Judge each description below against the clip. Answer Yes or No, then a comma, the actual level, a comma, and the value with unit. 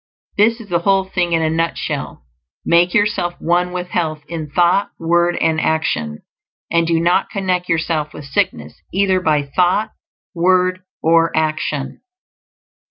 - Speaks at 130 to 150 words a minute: Yes, average, 145 wpm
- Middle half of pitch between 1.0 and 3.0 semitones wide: Yes, narrow, 2.5 semitones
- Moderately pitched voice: Yes, medium, 170 Hz